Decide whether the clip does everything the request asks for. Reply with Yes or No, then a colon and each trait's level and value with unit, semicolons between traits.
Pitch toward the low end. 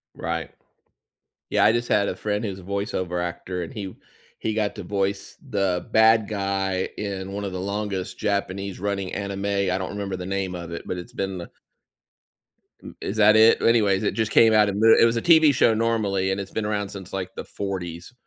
Yes: low, 100 Hz